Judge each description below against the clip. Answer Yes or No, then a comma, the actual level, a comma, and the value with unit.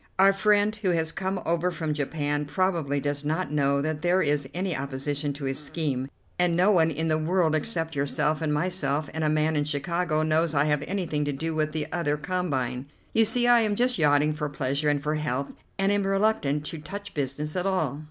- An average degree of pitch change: Yes, average, 3.8 semitones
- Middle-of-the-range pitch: Yes, medium, 155 Hz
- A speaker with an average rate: No, fast, 210 wpm